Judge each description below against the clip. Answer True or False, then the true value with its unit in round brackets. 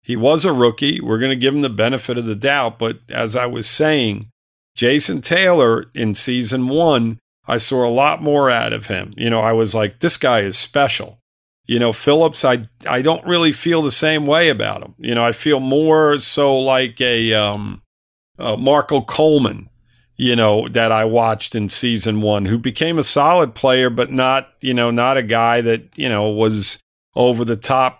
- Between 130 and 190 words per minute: False (200 wpm)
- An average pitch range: True (3.4 semitones)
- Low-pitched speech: True (120 Hz)